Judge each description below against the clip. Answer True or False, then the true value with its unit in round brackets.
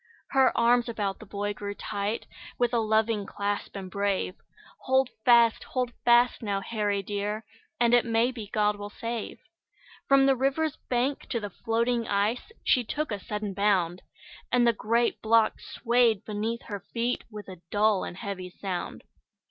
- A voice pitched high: True (220 Hz)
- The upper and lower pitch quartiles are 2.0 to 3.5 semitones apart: True (2.9 semitones)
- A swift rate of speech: False (165 wpm)